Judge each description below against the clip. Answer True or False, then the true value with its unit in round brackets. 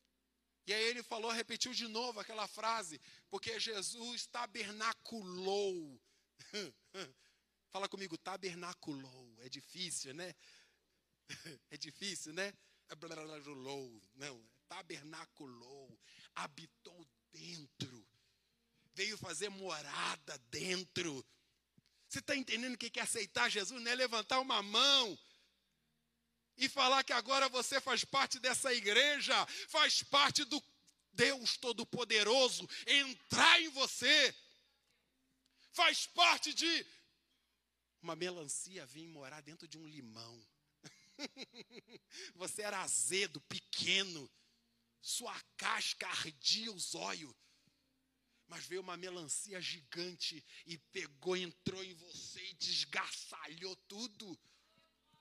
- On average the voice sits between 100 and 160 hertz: False (190 Hz)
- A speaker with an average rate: False (100 wpm)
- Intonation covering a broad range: True (7.3 semitones)